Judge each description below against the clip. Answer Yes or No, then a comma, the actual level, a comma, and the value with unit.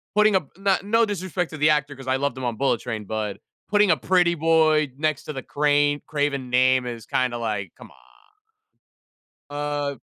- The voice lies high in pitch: No, medium, 145 Hz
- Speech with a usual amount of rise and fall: Yes, average, 4.0 semitones